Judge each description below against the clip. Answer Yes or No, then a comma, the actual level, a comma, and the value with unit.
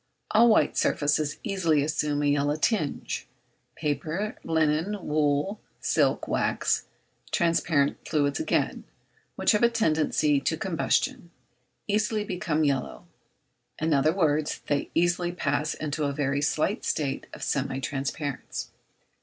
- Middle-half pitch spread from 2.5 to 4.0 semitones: Yes, average, 3.4 semitones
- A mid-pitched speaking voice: Yes, medium, 155 Hz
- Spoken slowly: Yes, slow, 120 wpm